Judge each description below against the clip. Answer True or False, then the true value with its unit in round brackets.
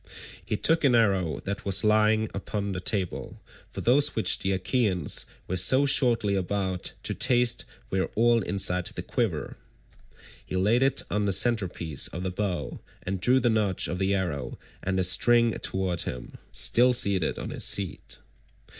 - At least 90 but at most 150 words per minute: False (165 wpm)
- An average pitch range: True (4.1 semitones)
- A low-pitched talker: True (100 Hz)